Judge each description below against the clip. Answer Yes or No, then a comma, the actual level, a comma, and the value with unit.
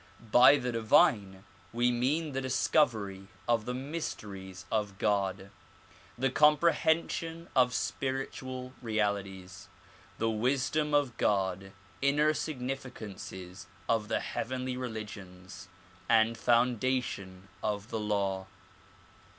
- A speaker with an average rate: No, slow, 100 wpm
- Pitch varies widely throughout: No, average, 4.7 semitones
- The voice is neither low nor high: No, low, 115 Hz